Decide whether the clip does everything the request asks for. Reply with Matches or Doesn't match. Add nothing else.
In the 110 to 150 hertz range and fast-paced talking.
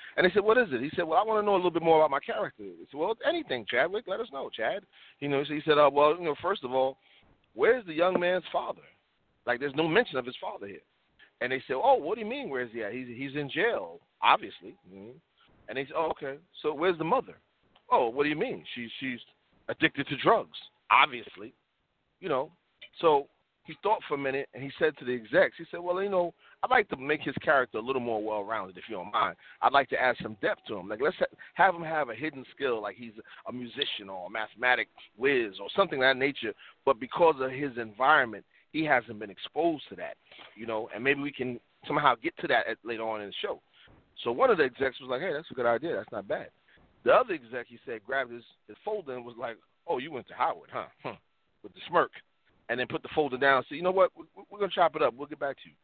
Matches